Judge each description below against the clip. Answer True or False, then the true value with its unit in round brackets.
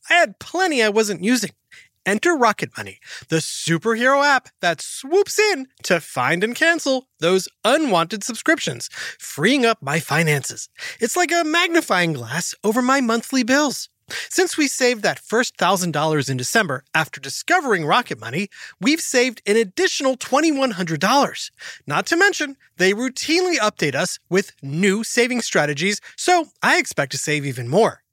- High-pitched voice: True (225 Hz)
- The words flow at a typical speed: True (150 wpm)